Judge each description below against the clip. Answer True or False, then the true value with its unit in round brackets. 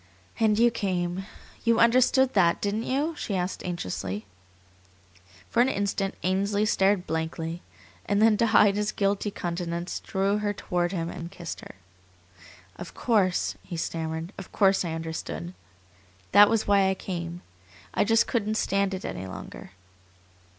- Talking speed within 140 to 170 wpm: True (150 wpm)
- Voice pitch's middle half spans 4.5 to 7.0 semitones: False (3.4 semitones)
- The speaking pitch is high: True (195 Hz)